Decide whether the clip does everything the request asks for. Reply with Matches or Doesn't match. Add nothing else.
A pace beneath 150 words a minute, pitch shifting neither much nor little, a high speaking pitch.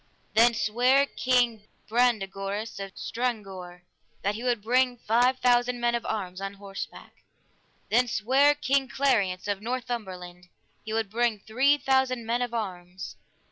Matches